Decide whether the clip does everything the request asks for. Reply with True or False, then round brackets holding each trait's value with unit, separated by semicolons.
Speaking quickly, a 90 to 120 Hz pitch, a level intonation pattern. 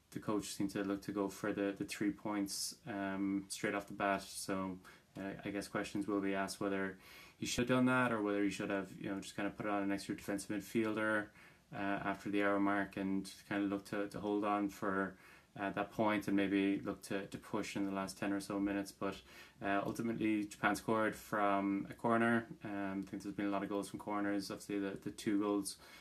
True (235 wpm; 100 Hz; 0.9 semitones)